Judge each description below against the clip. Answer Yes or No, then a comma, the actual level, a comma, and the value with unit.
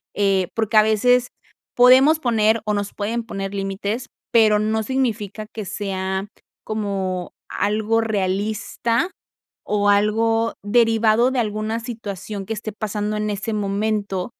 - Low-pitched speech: No, high, 215 Hz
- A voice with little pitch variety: Yes, narrow, 1.9 semitones